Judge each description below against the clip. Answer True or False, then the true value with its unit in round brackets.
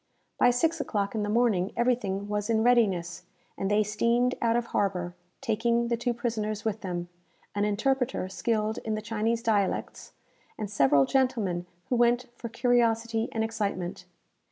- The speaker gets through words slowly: False (155 wpm)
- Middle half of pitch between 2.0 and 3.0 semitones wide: True (2.7 semitones)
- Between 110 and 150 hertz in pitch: False (225 Hz)